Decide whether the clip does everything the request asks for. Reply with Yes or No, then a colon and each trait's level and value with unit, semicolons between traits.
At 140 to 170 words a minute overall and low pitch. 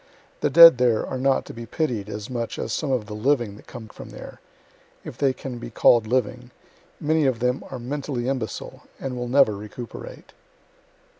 No: average, 195 wpm; low, 125 Hz